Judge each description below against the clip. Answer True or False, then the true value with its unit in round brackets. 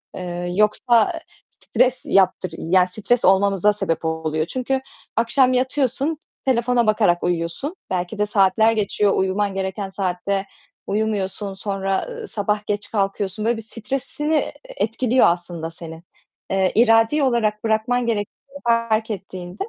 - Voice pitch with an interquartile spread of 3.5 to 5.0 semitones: True (3.8 semitones)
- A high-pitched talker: True (210 Hz)